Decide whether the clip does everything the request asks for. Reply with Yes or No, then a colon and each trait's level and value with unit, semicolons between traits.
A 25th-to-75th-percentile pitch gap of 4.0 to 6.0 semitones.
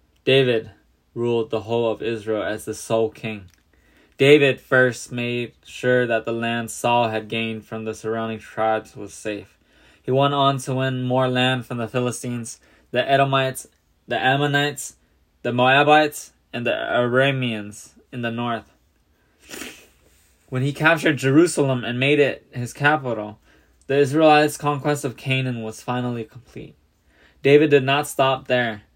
No: average, 3.6 semitones